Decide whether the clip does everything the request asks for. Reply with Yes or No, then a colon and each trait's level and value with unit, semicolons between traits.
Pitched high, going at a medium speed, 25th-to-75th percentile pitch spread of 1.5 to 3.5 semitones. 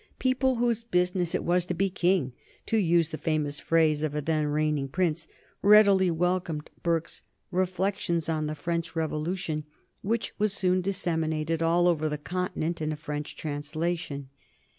No: medium, 165 Hz; average, 155 wpm; average, 3.1 semitones